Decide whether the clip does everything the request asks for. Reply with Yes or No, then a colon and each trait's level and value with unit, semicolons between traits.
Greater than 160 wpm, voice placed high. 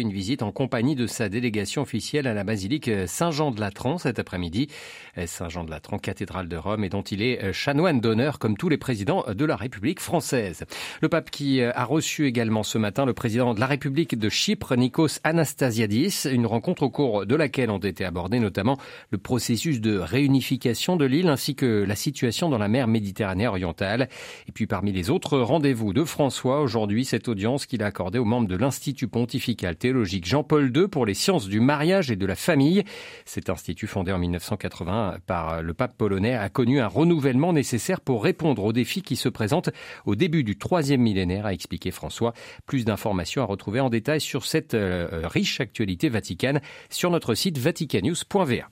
No: average, 185 wpm; low, 120 Hz